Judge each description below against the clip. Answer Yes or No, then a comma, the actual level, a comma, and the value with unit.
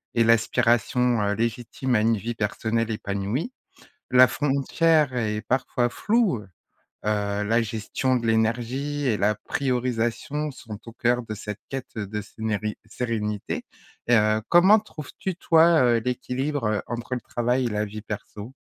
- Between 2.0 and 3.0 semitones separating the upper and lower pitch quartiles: No, average, 3.4 semitones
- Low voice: Yes, low, 115 Hz